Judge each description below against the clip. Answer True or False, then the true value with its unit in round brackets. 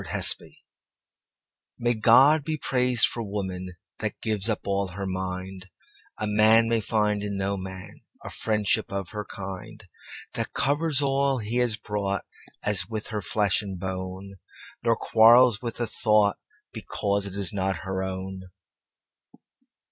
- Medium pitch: False (105 Hz)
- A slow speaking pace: True (125 wpm)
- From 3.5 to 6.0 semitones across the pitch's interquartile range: False (3.1 semitones)